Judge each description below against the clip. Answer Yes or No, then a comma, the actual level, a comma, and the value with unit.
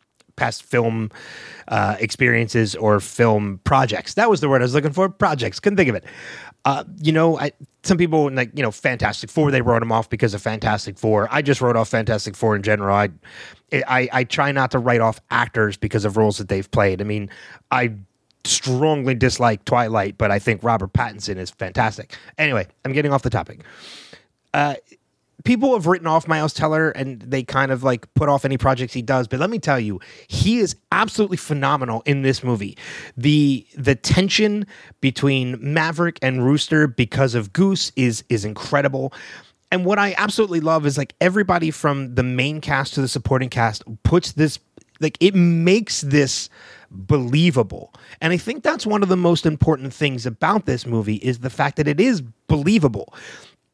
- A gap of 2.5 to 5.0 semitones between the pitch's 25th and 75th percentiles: No, wide, 5.4 semitones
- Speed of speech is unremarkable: Yes, average, 185 wpm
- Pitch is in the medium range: No, low, 130 Hz